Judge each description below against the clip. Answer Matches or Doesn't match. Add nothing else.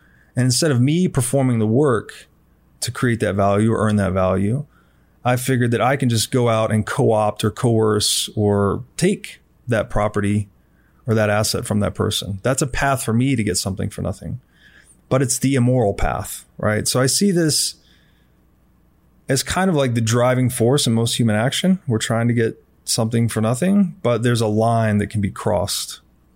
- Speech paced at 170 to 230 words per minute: Matches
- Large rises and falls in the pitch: Doesn't match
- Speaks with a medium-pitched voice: Doesn't match